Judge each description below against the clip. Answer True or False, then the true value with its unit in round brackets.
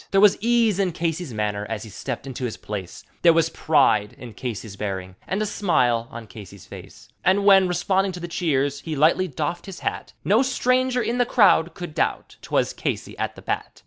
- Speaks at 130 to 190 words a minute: False (205 wpm)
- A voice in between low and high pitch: True (160 Hz)